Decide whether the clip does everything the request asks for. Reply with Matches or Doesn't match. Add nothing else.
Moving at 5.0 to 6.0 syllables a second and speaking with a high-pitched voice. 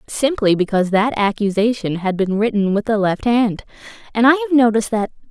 Matches